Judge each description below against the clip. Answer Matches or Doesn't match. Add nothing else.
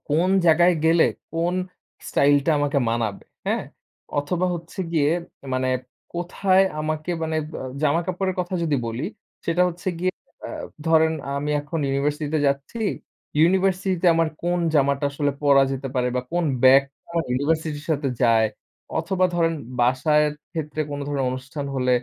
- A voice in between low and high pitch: Matches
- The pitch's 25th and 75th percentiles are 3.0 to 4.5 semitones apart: Matches